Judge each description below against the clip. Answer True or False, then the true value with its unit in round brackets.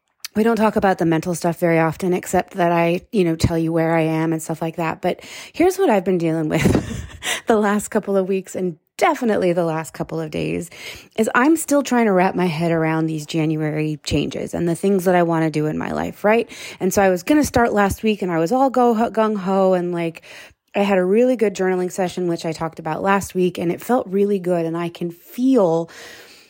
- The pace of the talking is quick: True (240 wpm)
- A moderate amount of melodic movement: True (4.2 semitones)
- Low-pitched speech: False (180 Hz)